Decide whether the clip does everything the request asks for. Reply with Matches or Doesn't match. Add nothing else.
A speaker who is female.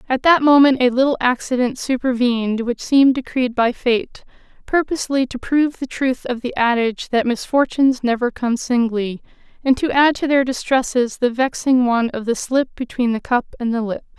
Matches